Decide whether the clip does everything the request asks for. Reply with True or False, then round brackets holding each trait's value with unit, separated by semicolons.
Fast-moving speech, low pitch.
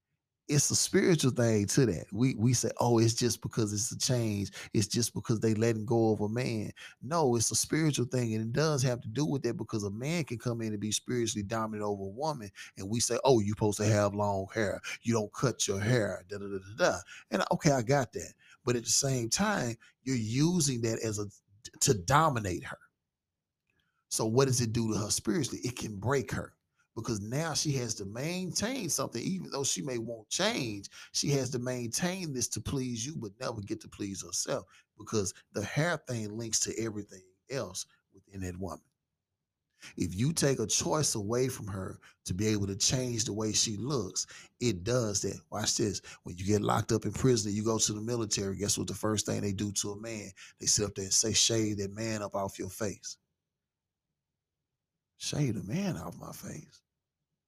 True (210 wpm; 115 Hz)